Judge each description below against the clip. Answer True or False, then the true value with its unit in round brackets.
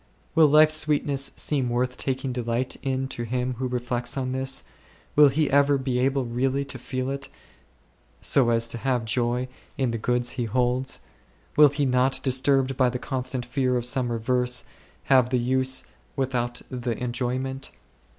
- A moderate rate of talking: True (165 wpm)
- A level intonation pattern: True (1.6 semitones)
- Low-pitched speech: True (130 Hz)